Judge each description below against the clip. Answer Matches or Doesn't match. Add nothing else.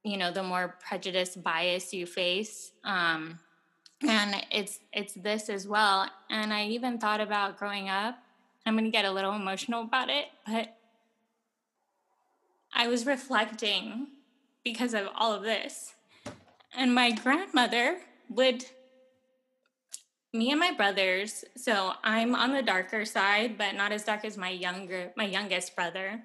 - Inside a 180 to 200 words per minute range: Doesn't match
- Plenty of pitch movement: Doesn't match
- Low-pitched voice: Doesn't match